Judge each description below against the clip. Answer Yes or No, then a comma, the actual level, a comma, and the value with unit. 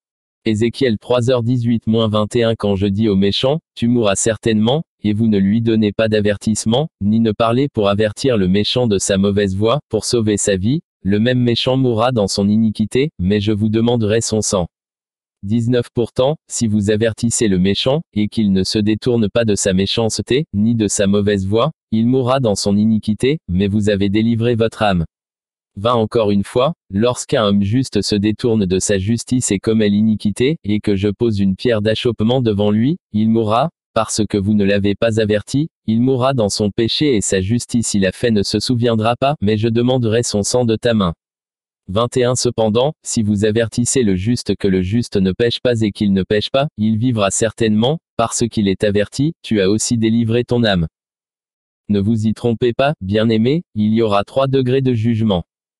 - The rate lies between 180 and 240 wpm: Yes, average, 190 wpm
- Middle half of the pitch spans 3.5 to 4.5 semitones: No, average, 2.7 semitones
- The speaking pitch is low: Yes, low, 110 Hz